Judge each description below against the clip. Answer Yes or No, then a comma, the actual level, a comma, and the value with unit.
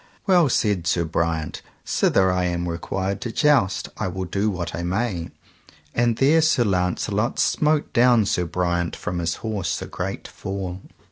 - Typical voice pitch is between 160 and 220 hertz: No, very low, 95 Hz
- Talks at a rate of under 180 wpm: Yes, average, 160 wpm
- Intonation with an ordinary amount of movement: Yes, average, 5.0 semitones